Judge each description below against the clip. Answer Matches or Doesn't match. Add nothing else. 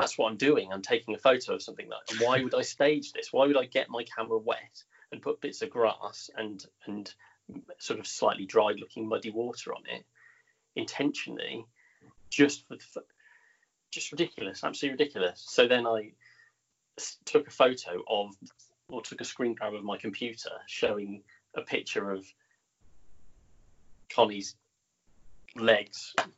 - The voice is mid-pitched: Doesn't match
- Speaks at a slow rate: Doesn't match